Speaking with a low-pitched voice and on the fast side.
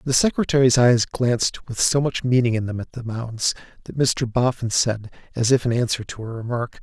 Yes: low, 120 Hz; fast, 210 wpm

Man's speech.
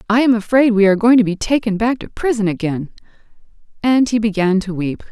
No: female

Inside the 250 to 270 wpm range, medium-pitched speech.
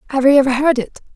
No: fast, 260 wpm; very high, 270 Hz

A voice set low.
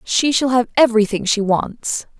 No: high, 230 Hz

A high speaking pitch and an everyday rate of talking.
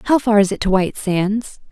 No: high, 210 Hz; fast, 245 wpm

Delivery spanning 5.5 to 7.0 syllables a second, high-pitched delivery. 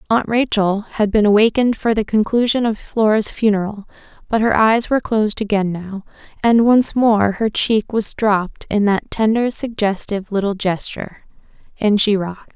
No: 5.0 syllables/s; high, 215 Hz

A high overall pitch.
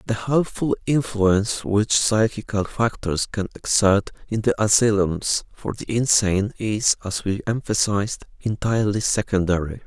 No: low, 105 Hz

